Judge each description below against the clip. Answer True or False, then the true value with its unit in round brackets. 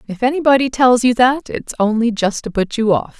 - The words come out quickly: True (225 wpm)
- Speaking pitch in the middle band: False (235 Hz)